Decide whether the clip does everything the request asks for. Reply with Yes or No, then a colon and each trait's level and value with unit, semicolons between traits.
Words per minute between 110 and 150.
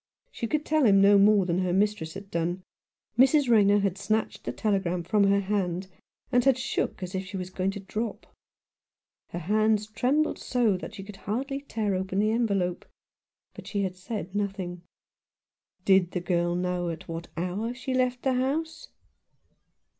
No: average, 175 wpm